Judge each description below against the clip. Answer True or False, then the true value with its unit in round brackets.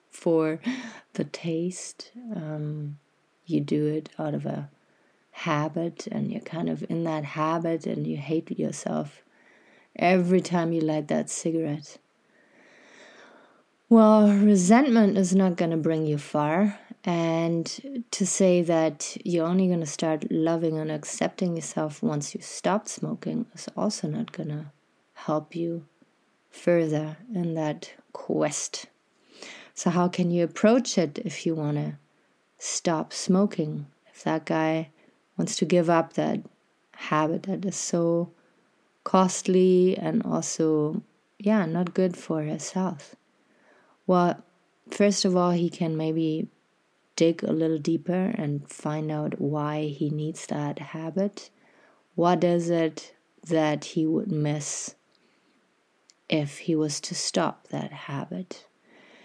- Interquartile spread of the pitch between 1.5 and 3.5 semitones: True (3.2 semitones)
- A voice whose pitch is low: False (165 Hz)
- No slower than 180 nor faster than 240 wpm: False (135 wpm)